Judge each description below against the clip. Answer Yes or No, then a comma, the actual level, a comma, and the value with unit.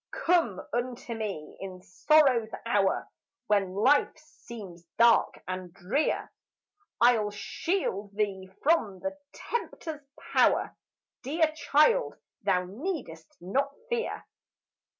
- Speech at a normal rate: No, slow, 100 wpm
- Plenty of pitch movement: Yes, wide, 7.6 semitones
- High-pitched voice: Yes, high, 230 Hz